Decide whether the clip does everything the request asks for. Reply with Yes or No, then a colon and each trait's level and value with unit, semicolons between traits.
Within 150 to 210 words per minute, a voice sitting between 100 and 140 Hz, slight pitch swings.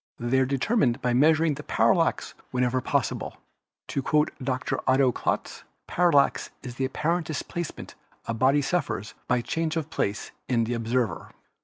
No: average, 160 wpm; low, 135 Hz; average, 4.0 semitones